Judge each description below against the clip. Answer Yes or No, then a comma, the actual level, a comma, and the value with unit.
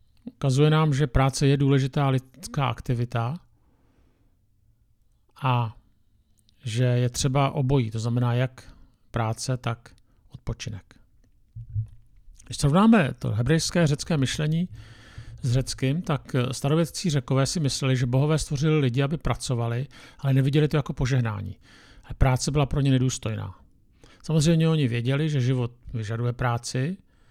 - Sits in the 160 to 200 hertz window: No, low, 130 Hz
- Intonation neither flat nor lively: Yes, average, 3.6 semitones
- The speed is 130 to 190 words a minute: No, average, 120 wpm